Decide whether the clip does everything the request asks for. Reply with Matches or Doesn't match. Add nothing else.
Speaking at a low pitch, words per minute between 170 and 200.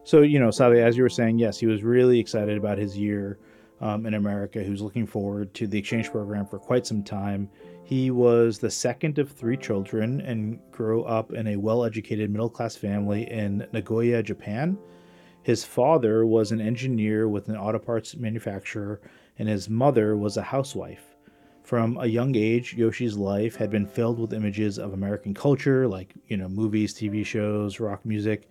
Matches